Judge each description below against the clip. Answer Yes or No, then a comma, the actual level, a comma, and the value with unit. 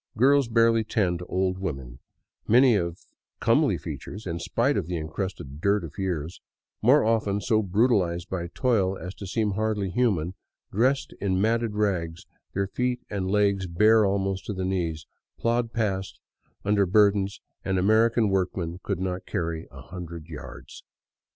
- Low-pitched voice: Yes, very low, 95 Hz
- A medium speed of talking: Yes, average, 155 wpm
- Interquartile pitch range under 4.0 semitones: Yes, average, 3.6 semitones